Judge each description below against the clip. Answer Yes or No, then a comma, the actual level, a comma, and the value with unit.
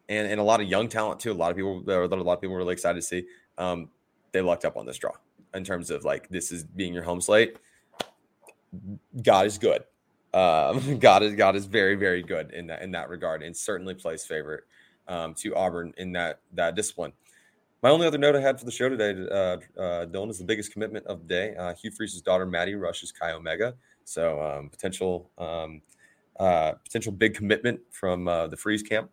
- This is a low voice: Yes, very low, 95 Hz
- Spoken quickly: Yes, fast, 220 wpm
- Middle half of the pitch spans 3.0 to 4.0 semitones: Yes, average, 3.6 semitones